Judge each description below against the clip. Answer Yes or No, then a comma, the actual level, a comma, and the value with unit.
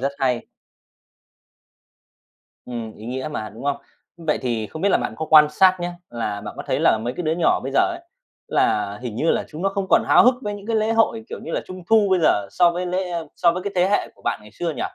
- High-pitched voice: No, medium, 160 Hz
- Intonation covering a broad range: Yes, wide, 7.6 semitones